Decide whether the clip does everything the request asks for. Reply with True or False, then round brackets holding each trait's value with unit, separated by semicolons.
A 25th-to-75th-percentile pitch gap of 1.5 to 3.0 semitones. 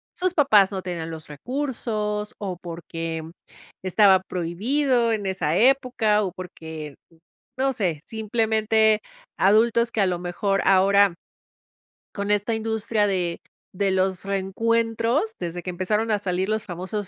False (3.6 semitones)